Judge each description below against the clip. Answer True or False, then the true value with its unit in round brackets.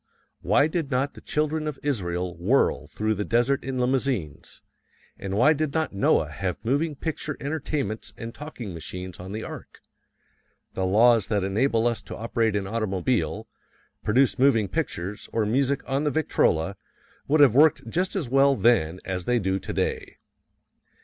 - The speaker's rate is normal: True (160 wpm)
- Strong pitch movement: True (6.2 semitones)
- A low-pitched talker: True (115 Hz)